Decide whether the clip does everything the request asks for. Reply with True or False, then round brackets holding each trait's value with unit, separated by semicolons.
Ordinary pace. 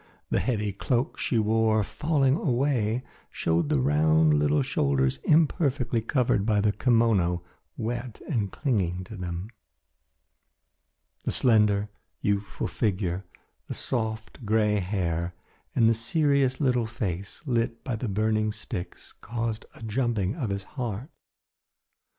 False (125 wpm)